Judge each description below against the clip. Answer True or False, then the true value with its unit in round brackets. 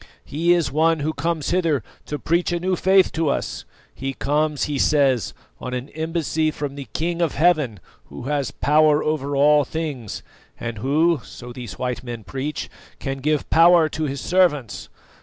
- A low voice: False (150 Hz)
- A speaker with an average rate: True (175 wpm)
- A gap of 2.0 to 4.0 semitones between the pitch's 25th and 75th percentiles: True (3.2 semitones)